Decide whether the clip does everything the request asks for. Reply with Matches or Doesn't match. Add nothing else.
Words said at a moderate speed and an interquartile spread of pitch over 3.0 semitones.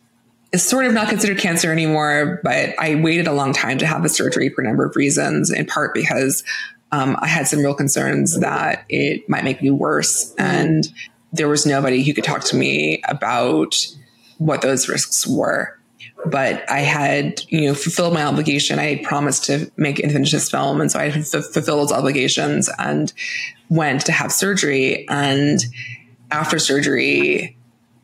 Matches